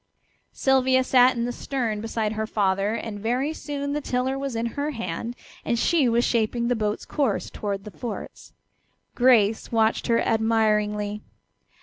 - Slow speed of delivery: No, average, 155 wpm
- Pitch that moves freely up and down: No, average, 3.2 semitones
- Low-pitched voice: No, high, 230 Hz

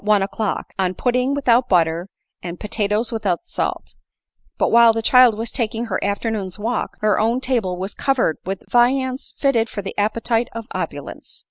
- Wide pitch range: No, average, 3.4 semitones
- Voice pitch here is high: Yes, high, 225 Hz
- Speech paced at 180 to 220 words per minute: No, average, 170 wpm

